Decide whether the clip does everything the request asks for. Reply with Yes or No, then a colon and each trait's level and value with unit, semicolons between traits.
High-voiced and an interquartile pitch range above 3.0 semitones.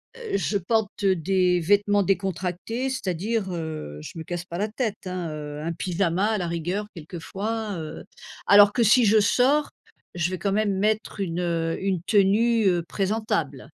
Yes: high, 195 Hz; average, 3.6 semitones